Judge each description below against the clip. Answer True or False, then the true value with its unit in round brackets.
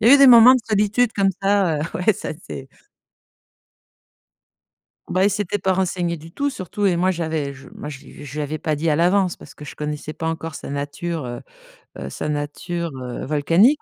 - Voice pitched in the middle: True (170 Hz)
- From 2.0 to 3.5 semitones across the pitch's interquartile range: False (4.9 semitones)